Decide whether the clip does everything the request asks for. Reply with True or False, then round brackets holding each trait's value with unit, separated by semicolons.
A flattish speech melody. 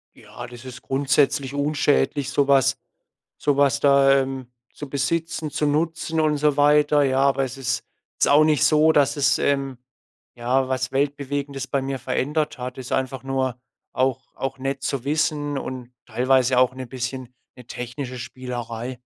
True (1.9 semitones)